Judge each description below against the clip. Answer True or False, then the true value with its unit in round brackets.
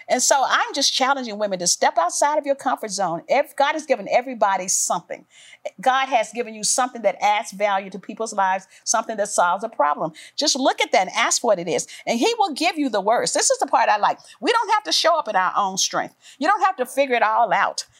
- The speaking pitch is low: False (260 Hz)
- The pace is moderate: False (250 wpm)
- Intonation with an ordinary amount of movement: False (6.9 semitones)